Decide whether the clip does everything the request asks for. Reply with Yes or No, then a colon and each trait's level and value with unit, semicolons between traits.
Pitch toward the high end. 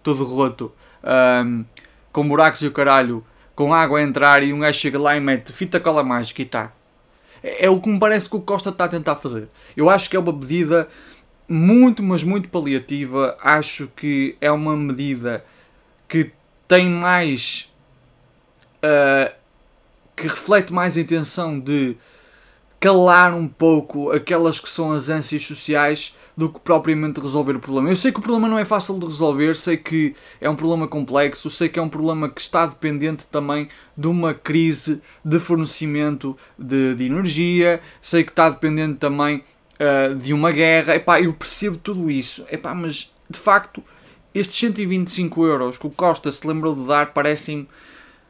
No: medium, 155 Hz